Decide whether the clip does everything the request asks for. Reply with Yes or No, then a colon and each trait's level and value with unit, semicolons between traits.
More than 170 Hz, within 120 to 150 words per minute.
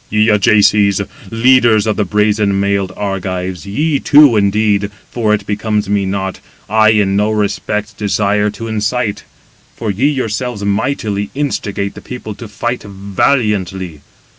No: low, 105 Hz; average, 140 wpm